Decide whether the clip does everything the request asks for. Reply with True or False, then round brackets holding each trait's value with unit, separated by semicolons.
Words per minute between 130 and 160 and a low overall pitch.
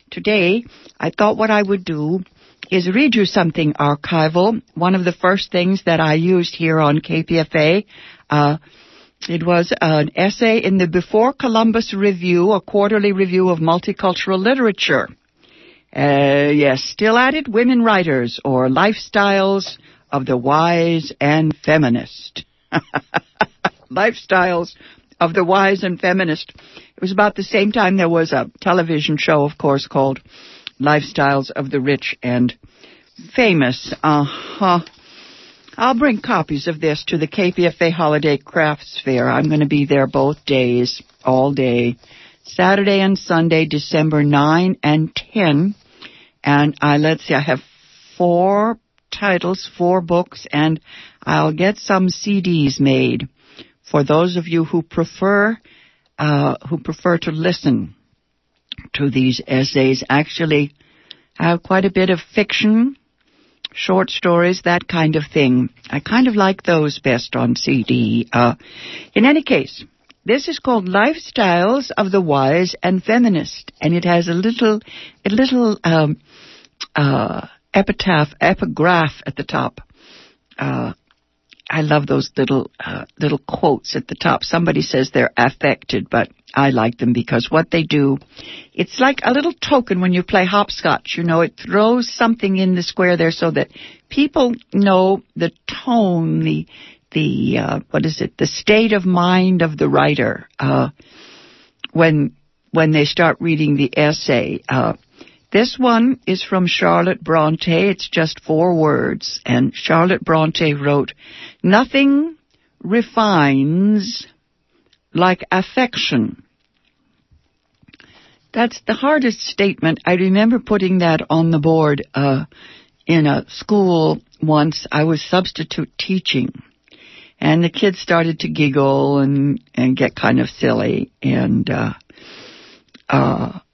False (140 wpm; 170 Hz)